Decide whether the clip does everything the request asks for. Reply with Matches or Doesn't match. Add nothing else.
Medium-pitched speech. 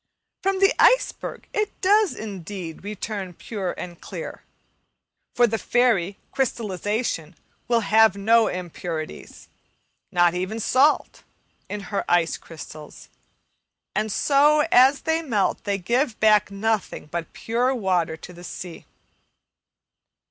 Doesn't match